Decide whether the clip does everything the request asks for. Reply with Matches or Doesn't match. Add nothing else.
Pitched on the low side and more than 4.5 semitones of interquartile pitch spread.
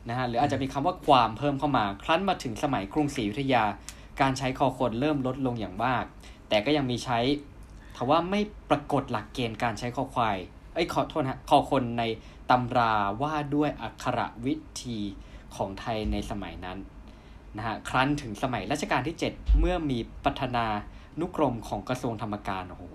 Matches